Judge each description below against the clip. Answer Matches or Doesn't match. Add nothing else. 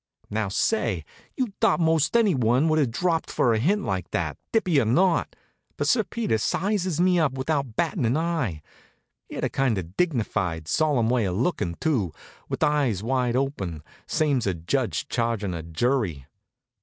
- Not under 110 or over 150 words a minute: Doesn't match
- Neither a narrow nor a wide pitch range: Doesn't match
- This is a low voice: Matches